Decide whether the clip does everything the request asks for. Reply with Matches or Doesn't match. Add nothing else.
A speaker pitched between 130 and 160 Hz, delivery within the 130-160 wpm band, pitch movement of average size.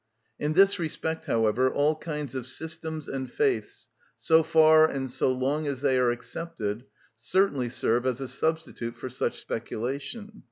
Matches